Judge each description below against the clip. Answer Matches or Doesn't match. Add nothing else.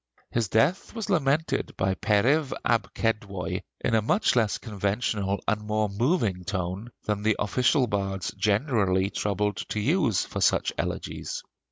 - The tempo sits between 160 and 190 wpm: Doesn't match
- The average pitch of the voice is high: Doesn't match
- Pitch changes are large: Doesn't match